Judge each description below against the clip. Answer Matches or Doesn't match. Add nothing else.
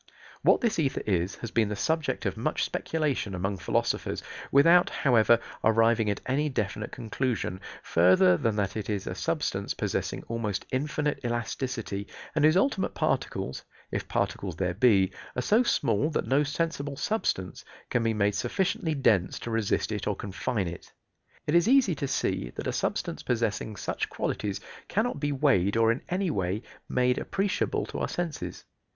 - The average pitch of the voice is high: Doesn't match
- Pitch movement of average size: Doesn't match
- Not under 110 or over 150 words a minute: Doesn't match